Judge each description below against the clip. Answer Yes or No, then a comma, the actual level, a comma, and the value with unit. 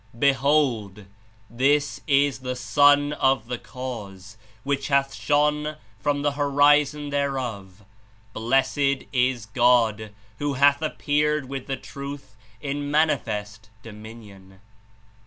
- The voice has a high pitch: No, low, 135 Hz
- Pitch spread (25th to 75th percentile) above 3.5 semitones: Yes, average, 4.0 semitones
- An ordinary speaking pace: No, slow, 105 wpm